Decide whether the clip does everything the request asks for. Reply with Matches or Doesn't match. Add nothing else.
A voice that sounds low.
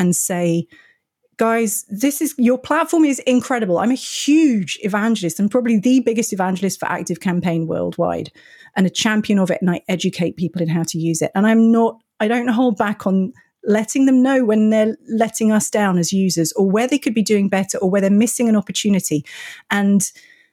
Doesn't match